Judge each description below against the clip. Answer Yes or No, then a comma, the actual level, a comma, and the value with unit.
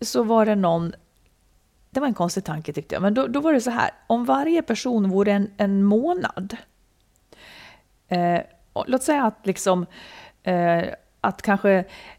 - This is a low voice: No, high, 205 Hz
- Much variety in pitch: Yes, wide, 5.7 semitones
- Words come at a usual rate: Yes, average, 165 wpm